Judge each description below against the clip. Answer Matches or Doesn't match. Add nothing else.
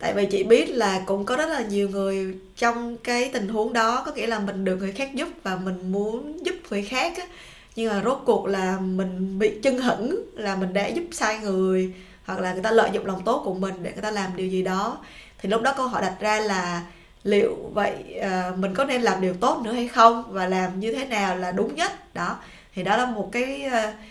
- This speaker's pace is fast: Doesn't match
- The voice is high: Matches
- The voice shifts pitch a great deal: Doesn't match